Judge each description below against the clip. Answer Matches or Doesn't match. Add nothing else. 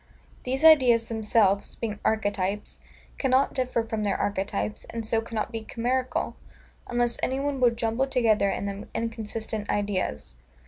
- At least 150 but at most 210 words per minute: Doesn't match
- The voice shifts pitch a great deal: Doesn't match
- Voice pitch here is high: Matches